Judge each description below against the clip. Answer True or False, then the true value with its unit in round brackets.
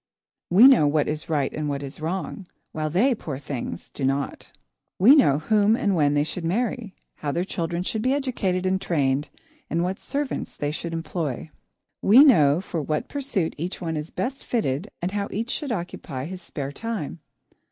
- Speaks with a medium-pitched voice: True (170 Hz)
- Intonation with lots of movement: True (6.1 semitones)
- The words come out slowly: False (185 wpm)